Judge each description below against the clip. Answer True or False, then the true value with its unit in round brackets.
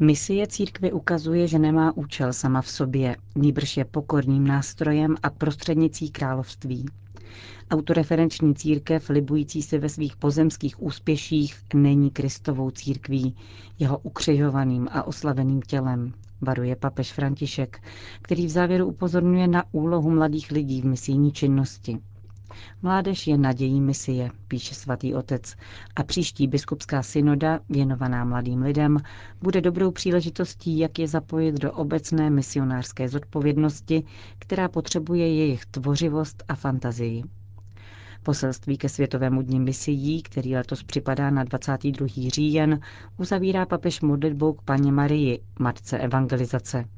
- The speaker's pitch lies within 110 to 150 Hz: True (140 Hz)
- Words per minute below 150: True (120 wpm)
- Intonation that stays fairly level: False (3.3 semitones)